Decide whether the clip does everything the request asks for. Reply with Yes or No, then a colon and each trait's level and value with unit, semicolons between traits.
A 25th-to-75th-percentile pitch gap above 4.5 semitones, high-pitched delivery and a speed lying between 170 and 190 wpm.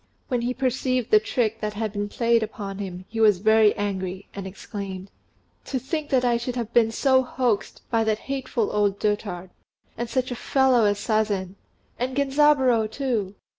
No: average, 3.7 semitones; high, 225 Hz; average, 175 wpm